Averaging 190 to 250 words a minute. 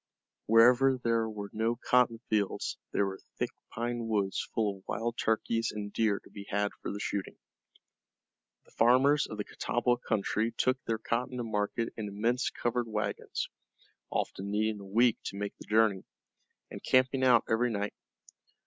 No: average, 165 wpm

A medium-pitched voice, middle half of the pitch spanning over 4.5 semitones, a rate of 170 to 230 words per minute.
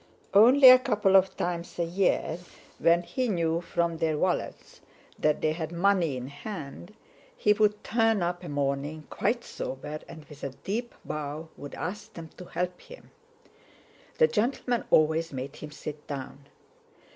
No: medium, 170 Hz; wide, 5.5 semitones; average, 155 wpm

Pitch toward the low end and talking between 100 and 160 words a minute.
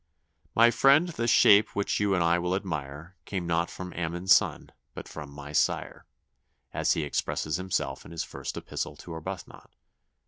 No: very low, 90 Hz; average, 170 wpm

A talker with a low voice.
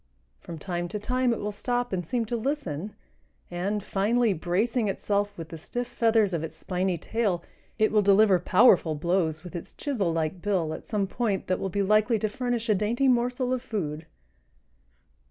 No: high, 205 Hz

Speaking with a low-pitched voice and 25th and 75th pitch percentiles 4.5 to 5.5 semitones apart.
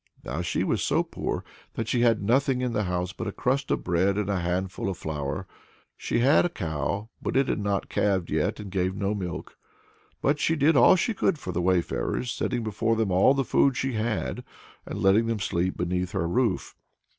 Yes: low, 100 Hz; average, 5.1 semitones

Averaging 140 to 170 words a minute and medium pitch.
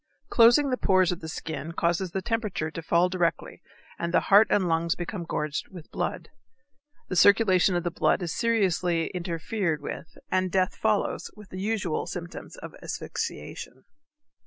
Yes: average, 160 wpm; medium, 180 Hz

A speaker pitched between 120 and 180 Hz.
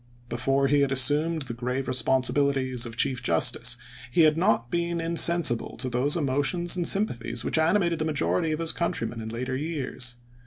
Yes: low, 135 Hz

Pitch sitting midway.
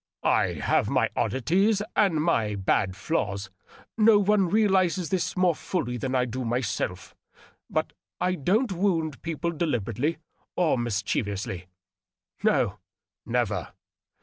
Yes: medium, 160 Hz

